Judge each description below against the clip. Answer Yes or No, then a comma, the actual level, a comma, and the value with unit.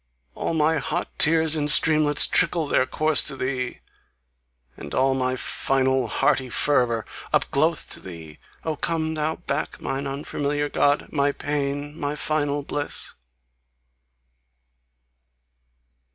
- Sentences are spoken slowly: Yes, slow, 125 wpm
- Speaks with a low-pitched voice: No, medium, 145 Hz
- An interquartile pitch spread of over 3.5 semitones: No, narrow, 2.4 semitones